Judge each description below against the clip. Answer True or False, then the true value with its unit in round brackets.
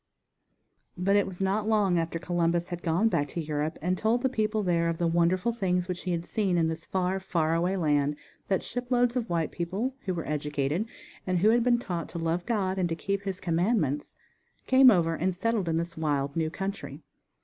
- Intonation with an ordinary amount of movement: True (3.5 semitones)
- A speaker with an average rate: False (215 wpm)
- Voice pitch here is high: False (180 Hz)